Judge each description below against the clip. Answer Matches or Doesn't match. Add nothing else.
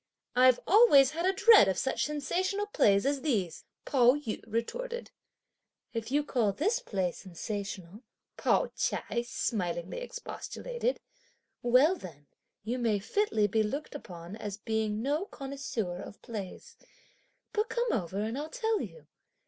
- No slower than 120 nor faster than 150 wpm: Matches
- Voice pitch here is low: Doesn't match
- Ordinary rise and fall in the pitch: Doesn't match